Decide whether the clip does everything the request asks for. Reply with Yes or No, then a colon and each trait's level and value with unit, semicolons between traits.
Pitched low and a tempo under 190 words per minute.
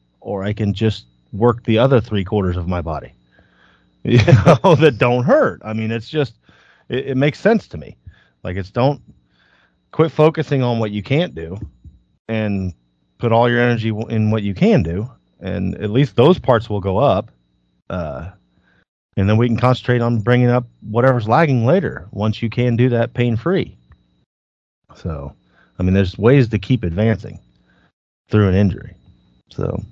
Yes: low, 110 Hz; average, 170 wpm